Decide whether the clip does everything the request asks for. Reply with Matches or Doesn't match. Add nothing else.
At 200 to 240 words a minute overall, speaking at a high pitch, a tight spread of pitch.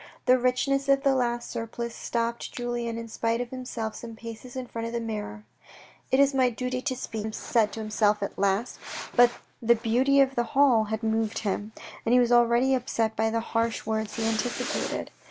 Matches